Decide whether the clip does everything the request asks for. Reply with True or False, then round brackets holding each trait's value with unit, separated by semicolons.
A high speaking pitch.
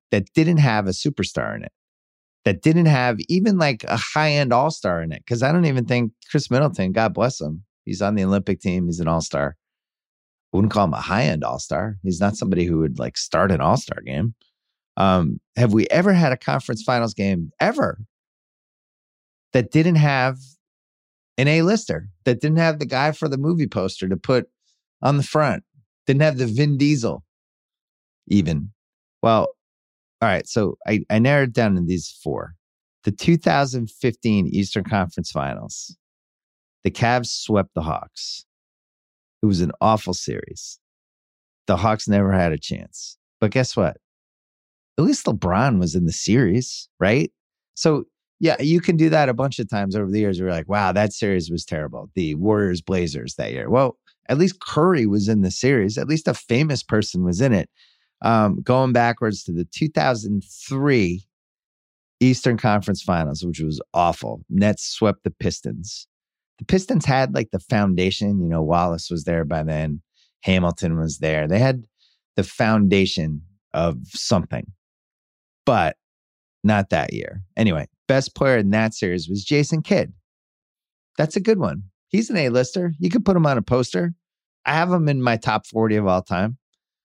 False (110 Hz)